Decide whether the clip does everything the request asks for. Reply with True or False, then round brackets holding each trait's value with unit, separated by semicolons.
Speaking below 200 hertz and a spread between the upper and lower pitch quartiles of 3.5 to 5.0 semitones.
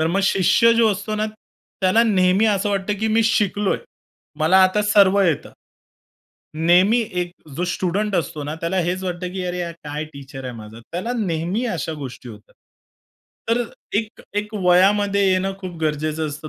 True (185 Hz; 4.2 semitones)